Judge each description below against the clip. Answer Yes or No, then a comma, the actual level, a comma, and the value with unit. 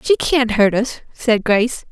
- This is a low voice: No, high, 235 Hz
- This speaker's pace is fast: No, average, 190 wpm